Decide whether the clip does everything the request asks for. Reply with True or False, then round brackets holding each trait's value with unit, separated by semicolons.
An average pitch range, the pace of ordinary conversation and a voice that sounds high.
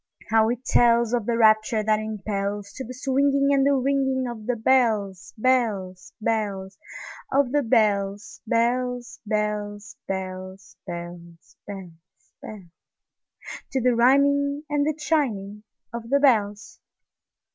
False (4.3 semitones; 105 wpm; 220 Hz)